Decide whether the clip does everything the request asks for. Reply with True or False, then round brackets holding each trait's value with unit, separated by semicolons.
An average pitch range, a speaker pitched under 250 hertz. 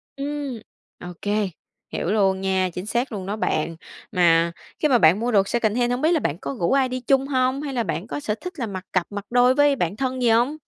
False (5.7 semitones; 235 Hz)